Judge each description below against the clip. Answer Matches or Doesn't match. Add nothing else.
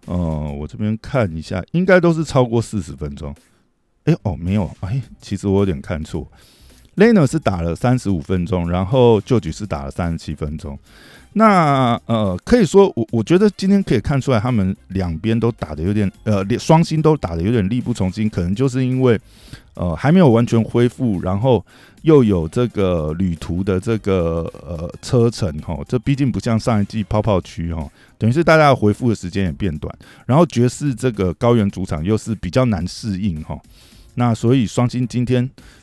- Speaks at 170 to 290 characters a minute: Matches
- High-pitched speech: Doesn't match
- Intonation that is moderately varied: Doesn't match